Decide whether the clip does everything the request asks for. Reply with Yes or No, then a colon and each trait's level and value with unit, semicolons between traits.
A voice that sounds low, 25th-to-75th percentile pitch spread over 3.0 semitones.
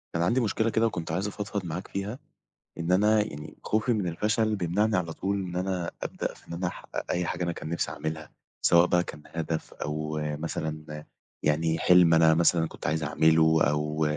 Yes: very low, 85 Hz; average, 3.7 semitones